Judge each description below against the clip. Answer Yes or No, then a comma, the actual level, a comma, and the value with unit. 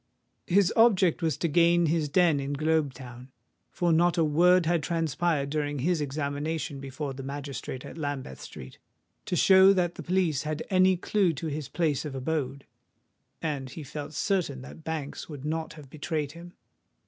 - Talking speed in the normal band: Yes, average, 170 wpm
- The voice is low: No, medium, 155 Hz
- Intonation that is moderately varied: Yes, average, 3.4 semitones